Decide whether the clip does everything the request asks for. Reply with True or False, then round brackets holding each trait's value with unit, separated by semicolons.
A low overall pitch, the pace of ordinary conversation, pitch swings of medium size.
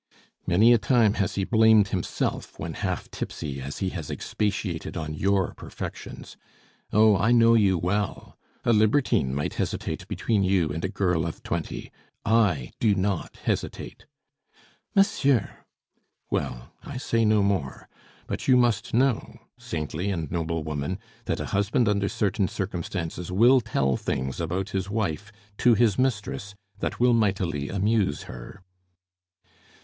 True (100 Hz; 145 wpm; 4.8 semitones)